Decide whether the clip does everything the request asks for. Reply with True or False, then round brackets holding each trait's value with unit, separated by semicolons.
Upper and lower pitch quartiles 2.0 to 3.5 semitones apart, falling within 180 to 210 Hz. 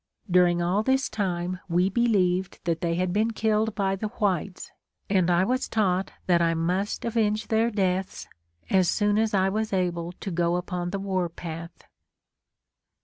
True (3.2 semitones; 190 Hz)